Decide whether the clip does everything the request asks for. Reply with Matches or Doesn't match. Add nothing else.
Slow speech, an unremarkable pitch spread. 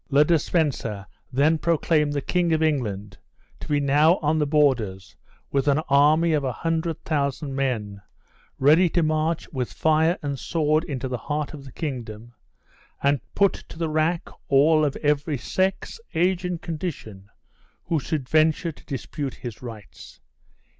Doesn't match